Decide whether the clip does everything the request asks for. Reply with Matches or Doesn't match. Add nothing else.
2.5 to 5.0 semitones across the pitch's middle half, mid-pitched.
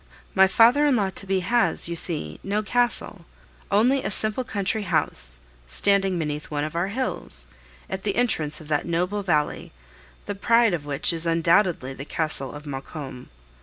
Doesn't match